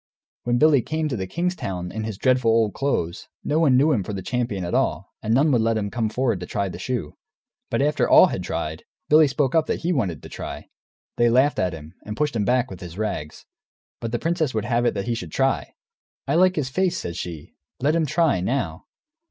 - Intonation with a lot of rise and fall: Yes, wide, 6.7 semitones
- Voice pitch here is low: Yes, low, 120 Hz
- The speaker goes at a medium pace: No, fast, 235 wpm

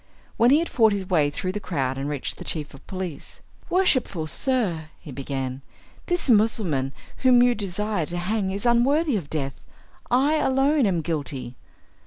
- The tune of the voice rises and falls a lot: Yes, wide, 8.7 semitones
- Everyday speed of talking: Yes, average, 170 wpm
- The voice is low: No, high, 190 Hz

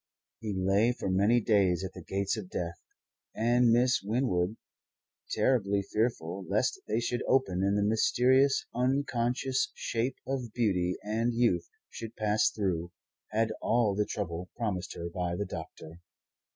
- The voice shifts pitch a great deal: No, average, 4.4 semitones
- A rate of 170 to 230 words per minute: No, average, 145 wpm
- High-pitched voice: No, low, 105 Hz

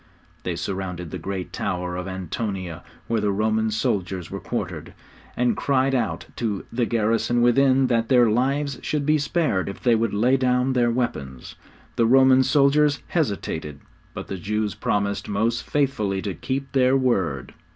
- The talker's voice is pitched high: No, low, 115 Hz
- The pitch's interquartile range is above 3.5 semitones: Yes, average, 5.1 semitones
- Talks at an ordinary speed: Yes, average, 160 wpm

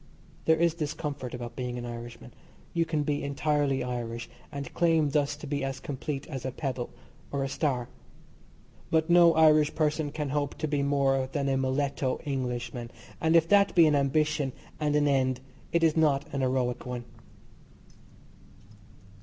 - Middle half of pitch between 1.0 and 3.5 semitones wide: Yes, average, 2.8 semitones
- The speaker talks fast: No, average, 170 wpm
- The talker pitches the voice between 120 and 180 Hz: Yes, medium, 140 Hz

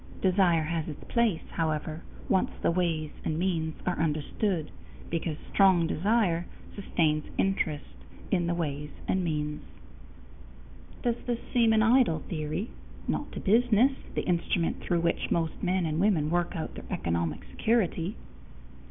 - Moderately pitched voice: Yes, medium, 170 Hz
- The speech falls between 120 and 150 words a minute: Yes, average, 140 wpm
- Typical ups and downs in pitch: Yes, average, 3.7 semitones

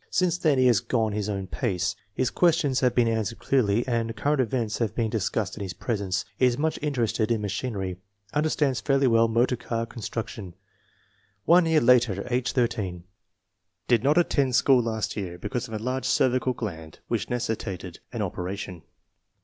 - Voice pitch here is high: No, low, 115 Hz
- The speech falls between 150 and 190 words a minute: Yes, average, 175 wpm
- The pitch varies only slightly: No, average, 3.9 semitones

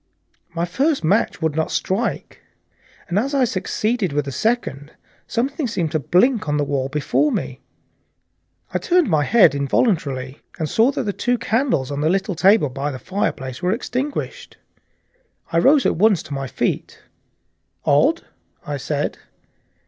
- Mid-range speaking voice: Yes, medium, 180 Hz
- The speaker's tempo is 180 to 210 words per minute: No, average, 155 wpm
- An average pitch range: No, wide, 8.6 semitones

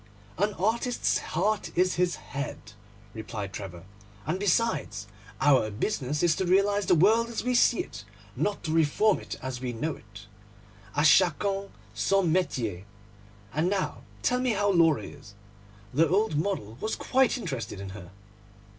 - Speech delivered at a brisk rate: No, average, 155 wpm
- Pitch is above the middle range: No, medium, 165 Hz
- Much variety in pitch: Yes, wide, 8.7 semitones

